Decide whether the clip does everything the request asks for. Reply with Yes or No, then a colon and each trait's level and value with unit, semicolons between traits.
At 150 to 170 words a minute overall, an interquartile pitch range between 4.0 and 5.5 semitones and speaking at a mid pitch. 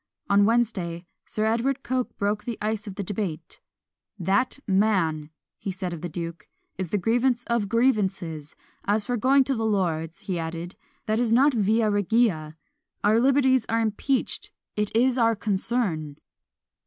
No: average, 155 wpm; average, 4.5 semitones; high, 210 Hz